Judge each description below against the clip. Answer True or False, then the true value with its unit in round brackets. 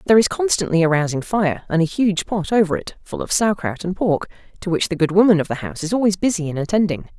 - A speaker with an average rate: False (260 wpm)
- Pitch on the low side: False (185 Hz)